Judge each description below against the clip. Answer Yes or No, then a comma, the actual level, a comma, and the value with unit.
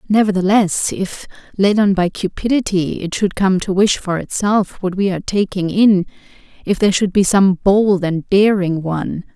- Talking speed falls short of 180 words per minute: Yes, average, 165 wpm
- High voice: Yes, high, 195 Hz